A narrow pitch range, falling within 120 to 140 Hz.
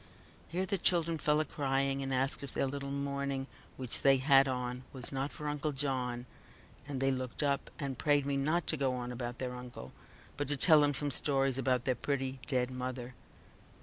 Yes: narrow, 2.0 semitones; low, 135 Hz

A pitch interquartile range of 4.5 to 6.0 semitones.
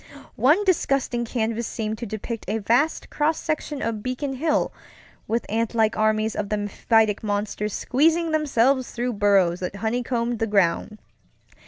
No: average, 3.6 semitones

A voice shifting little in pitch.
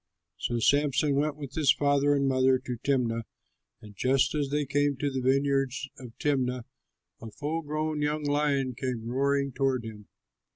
Yes: narrow, 2.2 semitones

